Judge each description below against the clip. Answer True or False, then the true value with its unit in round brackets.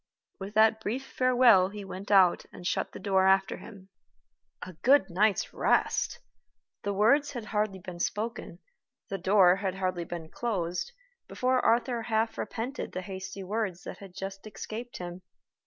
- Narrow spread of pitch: False (3.3 semitones)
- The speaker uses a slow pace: False (155 wpm)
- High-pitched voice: True (200 Hz)